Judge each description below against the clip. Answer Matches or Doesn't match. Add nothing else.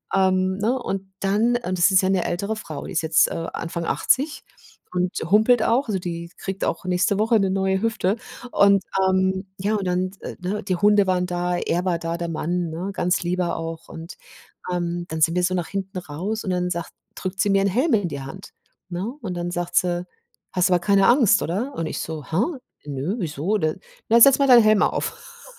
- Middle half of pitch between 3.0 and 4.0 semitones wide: Doesn't match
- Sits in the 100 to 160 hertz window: Doesn't match